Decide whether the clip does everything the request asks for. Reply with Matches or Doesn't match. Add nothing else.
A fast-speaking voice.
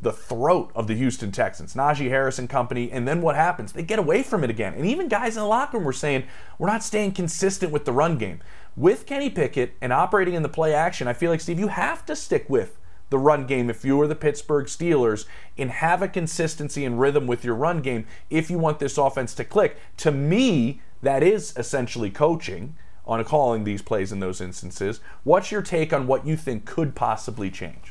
Matches